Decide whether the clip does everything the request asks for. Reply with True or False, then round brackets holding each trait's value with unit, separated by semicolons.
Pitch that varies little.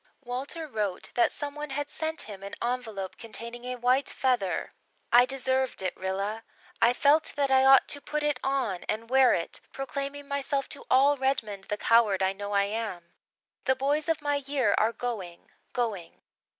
False (4.9 semitones)